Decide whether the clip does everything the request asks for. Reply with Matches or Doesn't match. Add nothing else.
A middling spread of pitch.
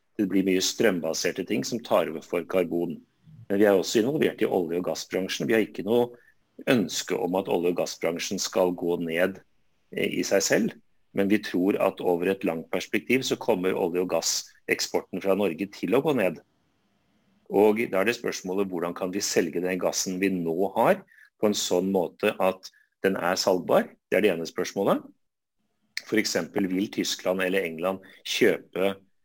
Doesn't match